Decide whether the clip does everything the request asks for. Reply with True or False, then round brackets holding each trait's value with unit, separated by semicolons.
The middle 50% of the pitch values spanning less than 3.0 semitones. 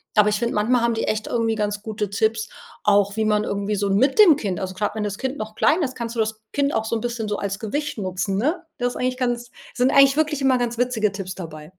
False (3.4 semitones)